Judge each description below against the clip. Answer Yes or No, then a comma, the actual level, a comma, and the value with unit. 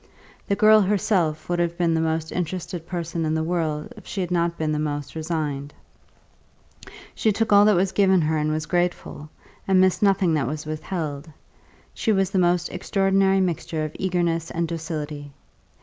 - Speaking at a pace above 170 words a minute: Yes, average, 180 wpm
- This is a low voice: No, medium, 170 Hz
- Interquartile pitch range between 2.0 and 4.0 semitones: Yes, average, 3.2 semitones